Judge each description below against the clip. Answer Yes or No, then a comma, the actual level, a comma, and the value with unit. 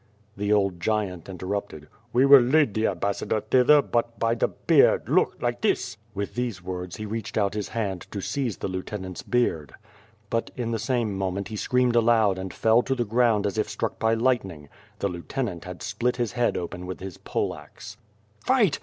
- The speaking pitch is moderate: No, low, 105 Hz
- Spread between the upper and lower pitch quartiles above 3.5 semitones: Yes, average, 4.1 semitones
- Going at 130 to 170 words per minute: No, average, 190 wpm